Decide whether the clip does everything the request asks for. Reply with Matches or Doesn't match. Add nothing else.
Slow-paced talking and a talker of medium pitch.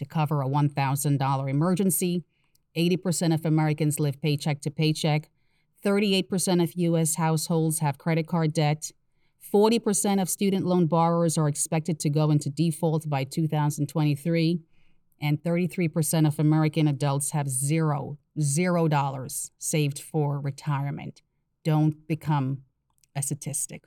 Matches